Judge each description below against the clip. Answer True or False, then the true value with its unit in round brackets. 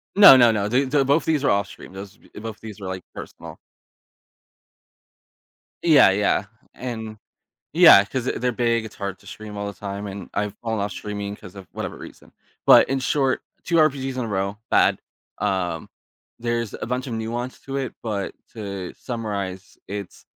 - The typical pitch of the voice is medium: False (110 Hz)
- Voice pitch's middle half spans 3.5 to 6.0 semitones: True (4.1 semitones)